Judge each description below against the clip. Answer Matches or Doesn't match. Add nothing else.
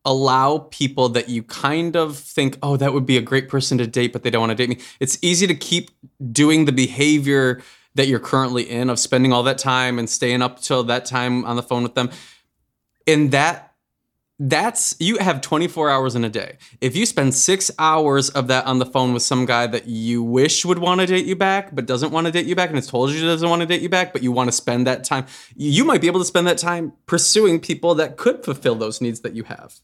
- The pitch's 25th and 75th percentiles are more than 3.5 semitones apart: Matches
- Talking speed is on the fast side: Matches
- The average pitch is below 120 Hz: Doesn't match